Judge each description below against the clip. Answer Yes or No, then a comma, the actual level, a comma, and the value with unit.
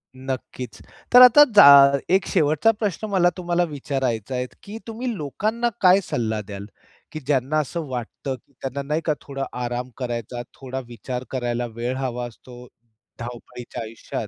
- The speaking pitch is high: No, low, 135 Hz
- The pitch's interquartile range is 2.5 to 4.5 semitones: No, average, 5.2 semitones